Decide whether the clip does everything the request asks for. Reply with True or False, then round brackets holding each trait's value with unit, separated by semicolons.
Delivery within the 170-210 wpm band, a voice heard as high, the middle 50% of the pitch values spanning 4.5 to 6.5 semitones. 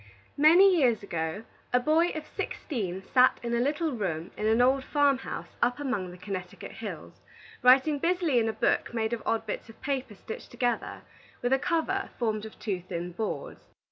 True (185 wpm; 245 Hz; 5.5 semitones)